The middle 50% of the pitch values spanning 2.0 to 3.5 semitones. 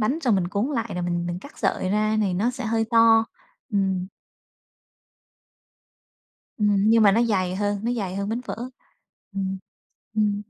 Yes: average, 2.9 semitones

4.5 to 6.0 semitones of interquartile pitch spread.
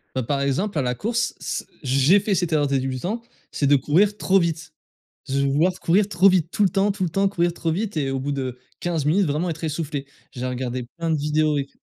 Yes: average, 5.2 semitones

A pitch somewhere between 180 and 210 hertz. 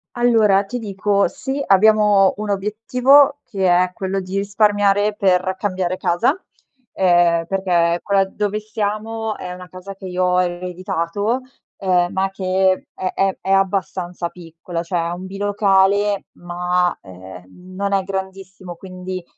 Yes: high, 190 Hz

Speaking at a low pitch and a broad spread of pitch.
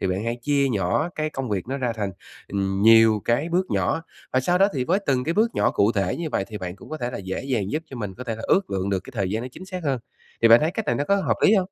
Yes: low, 125 Hz; wide, 7.5 semitones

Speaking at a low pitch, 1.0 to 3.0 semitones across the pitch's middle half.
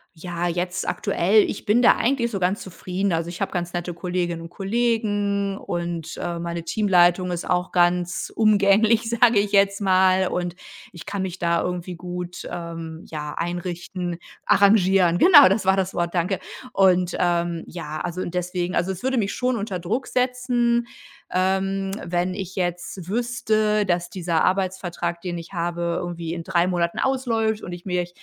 No: medium, 180 Hz; narrow, 2.5 semitones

